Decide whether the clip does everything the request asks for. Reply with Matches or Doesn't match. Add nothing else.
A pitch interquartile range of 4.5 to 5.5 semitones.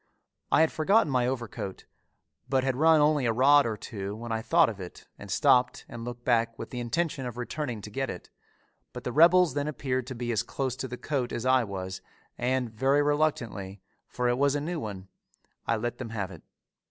Doesn't match